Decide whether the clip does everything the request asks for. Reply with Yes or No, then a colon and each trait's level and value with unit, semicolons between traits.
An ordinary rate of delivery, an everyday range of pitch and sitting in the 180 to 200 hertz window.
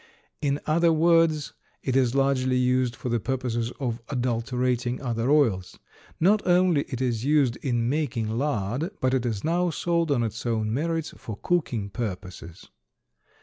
No: average, 150 wpm; average, 4.5 semitones; low, 130 Hz